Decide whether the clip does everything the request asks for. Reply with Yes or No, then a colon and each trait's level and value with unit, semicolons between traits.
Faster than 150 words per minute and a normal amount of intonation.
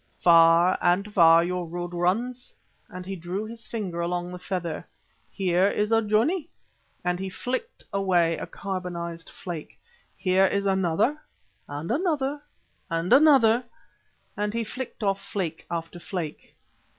No: average, 140 wpm; average, 4.1 semitones